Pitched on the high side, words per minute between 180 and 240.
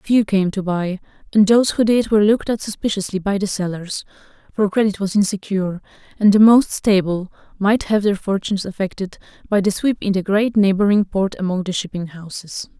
Yes: high, 200 Hz; average, 190 wpm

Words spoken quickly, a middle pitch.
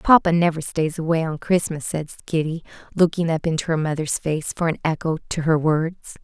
No: average, 190 wpm; medium, 160 Hz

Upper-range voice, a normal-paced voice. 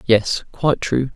No: low, 125 Hz; average, 155 wpm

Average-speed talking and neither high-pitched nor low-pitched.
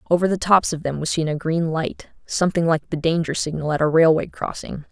No: fast, 230 wpm; medium, 165 Hz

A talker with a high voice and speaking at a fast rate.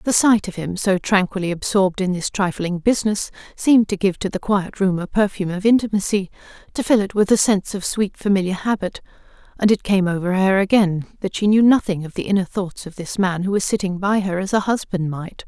Yes: high, 195 Hz; fast, 225 wpm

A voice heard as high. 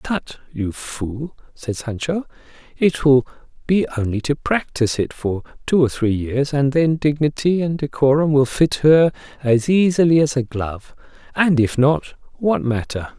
No: medium, 140 Hz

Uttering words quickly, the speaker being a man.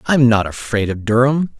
Yes: fast, 225 wpm; male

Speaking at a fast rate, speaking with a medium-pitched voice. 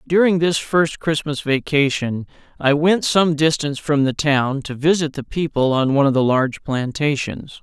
No: average, 175 wpm; medium, 145 Hz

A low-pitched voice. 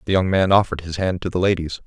Yes: very low, 90 Hz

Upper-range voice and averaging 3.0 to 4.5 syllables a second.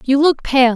Yes: very high, 270 Hz; 4.3 syllables/s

